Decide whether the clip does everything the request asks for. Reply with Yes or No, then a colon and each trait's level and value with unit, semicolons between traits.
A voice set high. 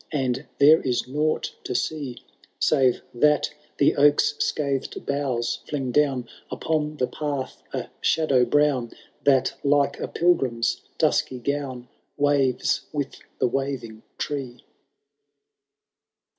No: medium, 140 Hz